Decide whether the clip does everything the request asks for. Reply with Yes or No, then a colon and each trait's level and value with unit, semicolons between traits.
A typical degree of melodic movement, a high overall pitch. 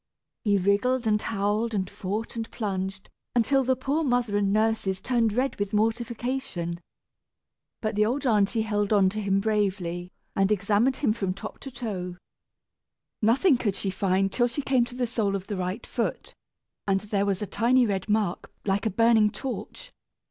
Yes: average, 3.3 semitones; high, 210 Hz